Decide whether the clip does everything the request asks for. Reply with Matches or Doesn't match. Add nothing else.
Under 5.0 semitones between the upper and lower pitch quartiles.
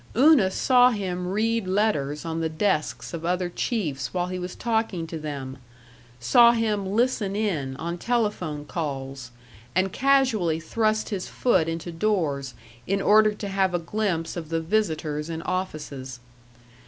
Doesn't match